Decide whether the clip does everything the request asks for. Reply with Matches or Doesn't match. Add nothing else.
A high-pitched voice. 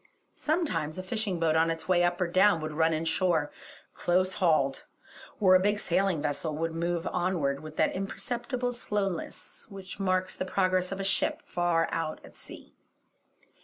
Doesn't match